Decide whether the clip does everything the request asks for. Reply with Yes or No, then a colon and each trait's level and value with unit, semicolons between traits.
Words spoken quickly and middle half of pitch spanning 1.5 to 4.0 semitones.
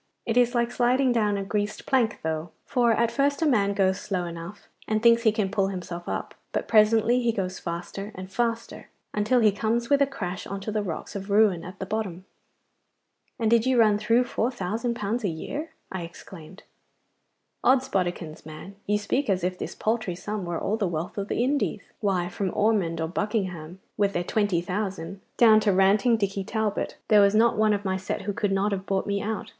Yes: fast, 210 wpm; average, 3.4 semitones